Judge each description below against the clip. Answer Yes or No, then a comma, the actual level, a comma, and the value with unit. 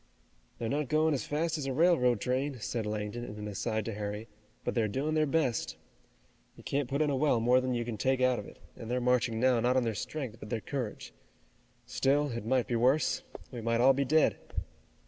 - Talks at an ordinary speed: No, fast, 225 wpm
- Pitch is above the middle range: No, low, 125 Hz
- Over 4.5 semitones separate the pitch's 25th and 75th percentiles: No, average, 3.4 semitones